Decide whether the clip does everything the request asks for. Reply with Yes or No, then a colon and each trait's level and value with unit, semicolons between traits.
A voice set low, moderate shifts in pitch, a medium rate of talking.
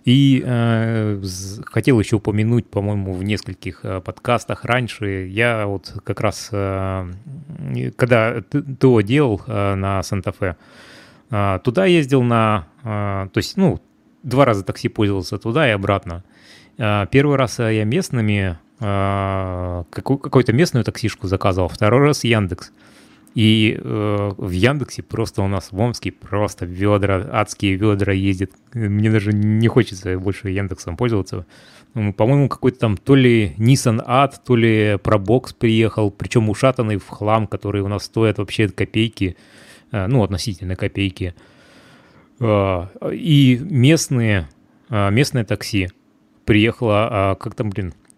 Yes: low, 105 Hz; average, 3.5 semitones; average, 135 wpm